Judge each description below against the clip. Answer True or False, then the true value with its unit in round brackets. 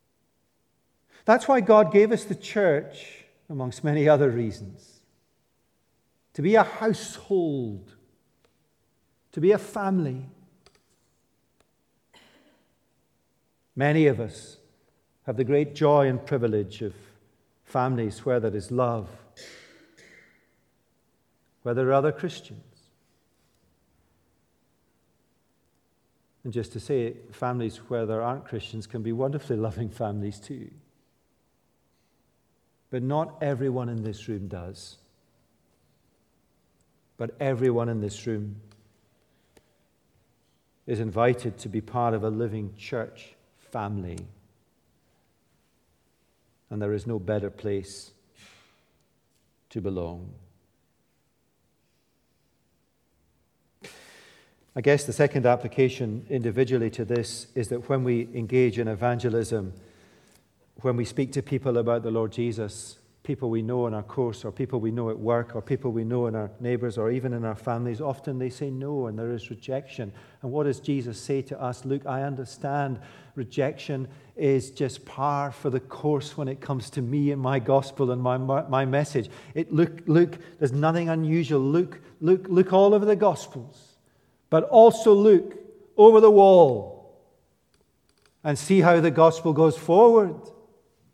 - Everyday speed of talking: False (130 wpm)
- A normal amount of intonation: True (4.3 semitones)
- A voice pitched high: False (125 Hz)